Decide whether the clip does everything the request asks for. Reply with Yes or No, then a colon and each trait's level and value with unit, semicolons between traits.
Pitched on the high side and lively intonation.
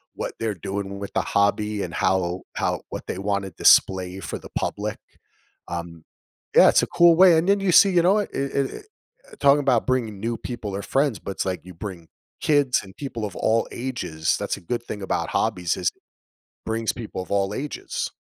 No: low, 105 Hz; wide, 6.3 semitones